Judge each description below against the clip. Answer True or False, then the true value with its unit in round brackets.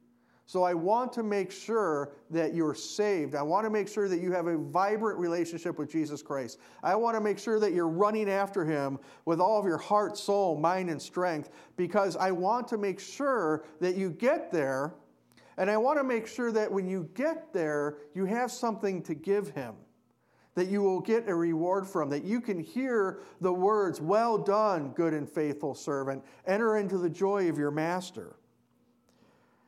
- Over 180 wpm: True (190 wpm)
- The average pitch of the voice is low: False (185 Hz)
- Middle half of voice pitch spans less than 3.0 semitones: False (4.7 semitones)